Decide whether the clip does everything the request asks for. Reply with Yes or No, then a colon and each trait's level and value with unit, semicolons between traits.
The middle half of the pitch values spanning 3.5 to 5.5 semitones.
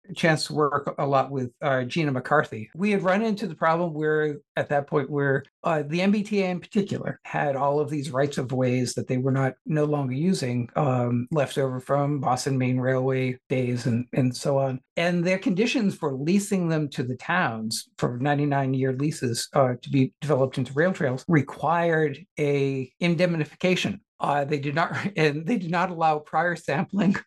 Yes: average, 4.4 semitones